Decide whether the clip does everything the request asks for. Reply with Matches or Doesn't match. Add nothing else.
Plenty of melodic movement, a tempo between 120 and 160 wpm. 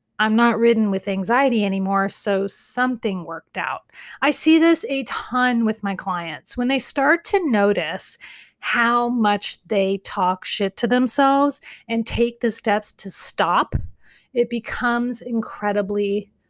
Doesn't match